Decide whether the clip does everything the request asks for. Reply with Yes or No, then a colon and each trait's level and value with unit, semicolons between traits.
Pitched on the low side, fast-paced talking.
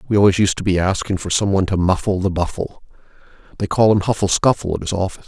Yes: very low, 95 Hz; fast, 240 wpm